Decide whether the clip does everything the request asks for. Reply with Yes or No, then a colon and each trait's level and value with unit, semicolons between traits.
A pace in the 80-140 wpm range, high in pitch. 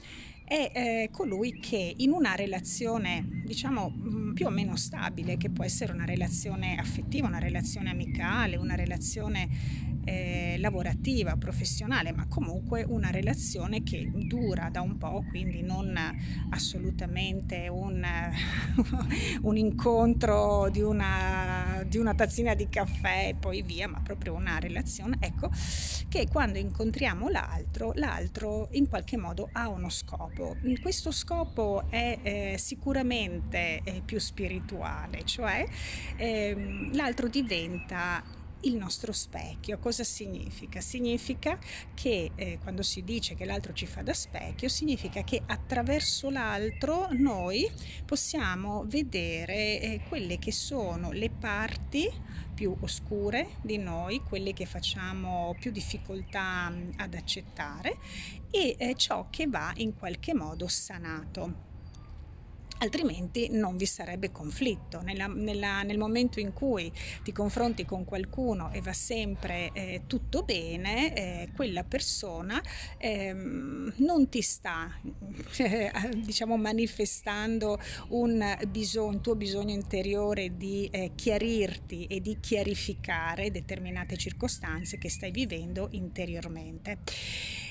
Yes: average, 120 wpm; high, 200 Hz